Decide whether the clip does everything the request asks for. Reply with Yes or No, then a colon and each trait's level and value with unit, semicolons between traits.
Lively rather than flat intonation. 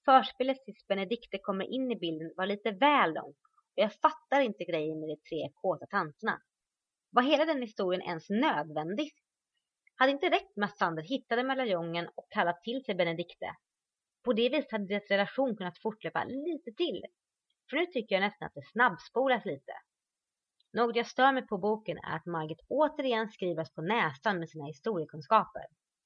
Yes: wide, 6.9 semitones